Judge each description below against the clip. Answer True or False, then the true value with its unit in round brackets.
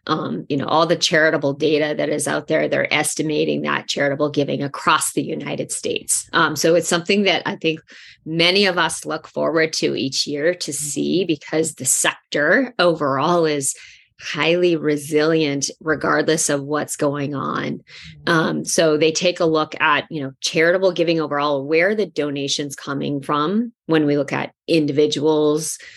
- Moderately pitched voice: True (155 Hz)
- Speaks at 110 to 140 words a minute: False (165 wpm)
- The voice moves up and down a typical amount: False (2.3 semitones)